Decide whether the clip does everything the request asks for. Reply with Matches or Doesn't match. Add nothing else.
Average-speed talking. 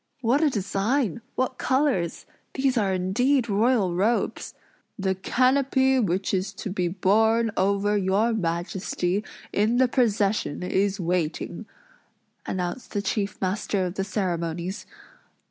Doesn't match